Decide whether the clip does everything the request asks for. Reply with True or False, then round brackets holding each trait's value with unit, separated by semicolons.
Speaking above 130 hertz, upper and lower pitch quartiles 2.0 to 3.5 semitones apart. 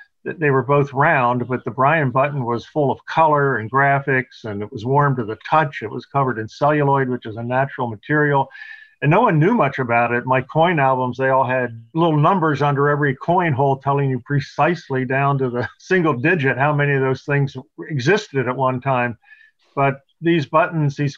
True (140 Hz; 2.4 semitones)